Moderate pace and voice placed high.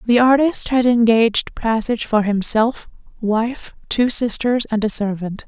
Yes: average, 145 wpm; high, 230 Hz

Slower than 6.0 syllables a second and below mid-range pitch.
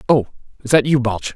Yes: 5.4 syllables/s; low, 125 Hz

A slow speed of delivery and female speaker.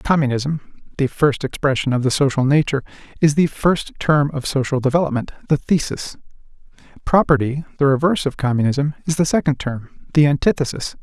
No: slow, 130 wpm; male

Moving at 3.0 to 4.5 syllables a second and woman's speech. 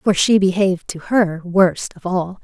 Yes: 4.3 syllables/s; female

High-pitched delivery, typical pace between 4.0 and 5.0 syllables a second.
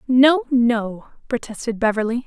Yes: high, 235 Hz; 4.3 syllables/s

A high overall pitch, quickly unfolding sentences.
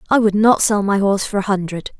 Yes: high, 200 Hz; fast, 270 wpm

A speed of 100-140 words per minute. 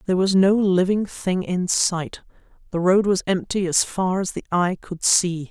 No: average, 195 wpm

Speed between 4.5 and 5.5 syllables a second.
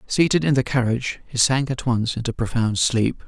Yes: 5.2 syllables/s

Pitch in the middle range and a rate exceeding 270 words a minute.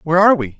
Yes: medium, 170 Hz; fast, 300 wpm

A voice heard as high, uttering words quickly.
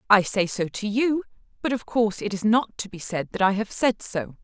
Yes: high, 210 Hz; fast, 255 wpm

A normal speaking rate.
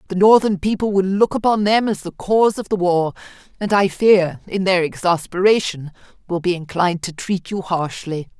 Yes: average, 185 wpm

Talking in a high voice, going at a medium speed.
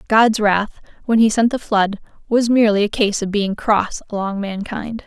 Yes: high, 210 Hz; average, 190 wpm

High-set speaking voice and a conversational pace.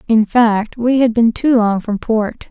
No: high, 225 Hz; fast, 215 wpm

